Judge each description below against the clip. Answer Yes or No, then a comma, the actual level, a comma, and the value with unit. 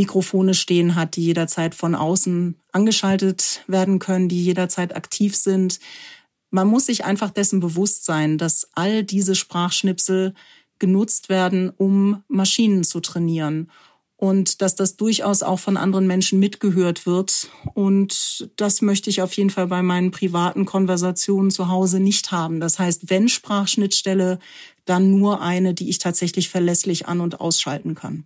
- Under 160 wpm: Yes, average, 150 wpm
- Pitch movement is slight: Yes, narrow, 1.9 semitones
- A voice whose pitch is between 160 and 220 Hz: Yes, high, 190 Hz